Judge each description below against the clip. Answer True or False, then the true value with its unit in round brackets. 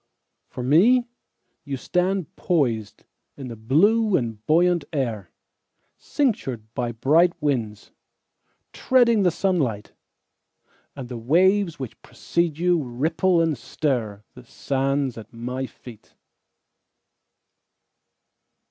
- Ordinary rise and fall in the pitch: False (6.9 semitones)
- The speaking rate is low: True (80 wpm)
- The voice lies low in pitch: False (145 Hz)